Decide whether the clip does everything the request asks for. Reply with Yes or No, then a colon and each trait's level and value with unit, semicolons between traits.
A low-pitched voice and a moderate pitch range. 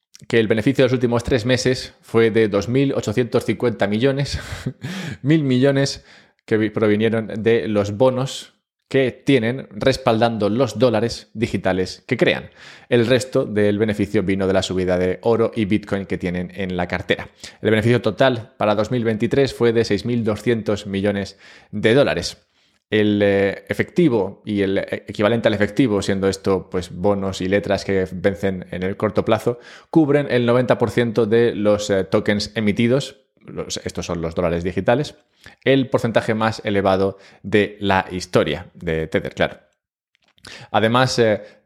Yes: low, 110 Hz; average, 3.6 semitones